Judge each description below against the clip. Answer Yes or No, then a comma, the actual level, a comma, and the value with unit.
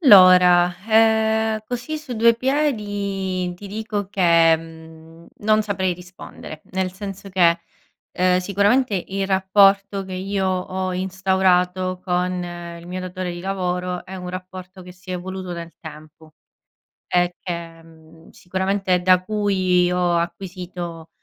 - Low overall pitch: No, medium, 185 Hz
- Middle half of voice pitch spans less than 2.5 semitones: Yes, narrow, 1.9 semitones